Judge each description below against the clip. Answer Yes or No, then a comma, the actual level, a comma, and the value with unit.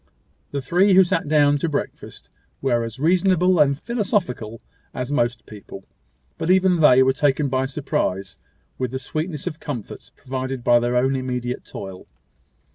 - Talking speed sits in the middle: Yes, average, 155 wpm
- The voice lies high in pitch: No, low, 135 Hz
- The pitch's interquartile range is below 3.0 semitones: No, average, 4.6 semitones